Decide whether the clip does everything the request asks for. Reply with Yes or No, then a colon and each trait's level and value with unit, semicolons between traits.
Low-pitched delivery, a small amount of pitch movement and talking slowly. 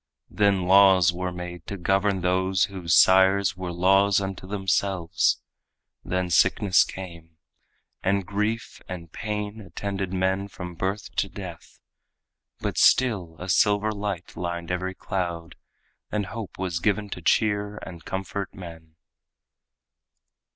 Yes: very low, 95 Hz; narrow, 2.2 semitones; slow, 125 wpm